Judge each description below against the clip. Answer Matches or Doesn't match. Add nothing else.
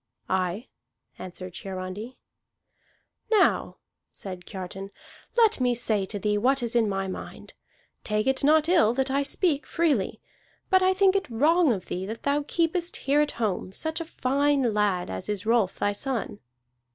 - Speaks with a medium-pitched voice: Doesn't match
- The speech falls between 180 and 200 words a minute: Doesn't match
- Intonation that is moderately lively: Doesn't match